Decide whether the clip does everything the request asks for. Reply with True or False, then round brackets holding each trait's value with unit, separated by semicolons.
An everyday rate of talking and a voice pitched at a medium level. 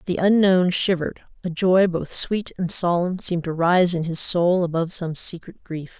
True (190 wpm; 175 Hz)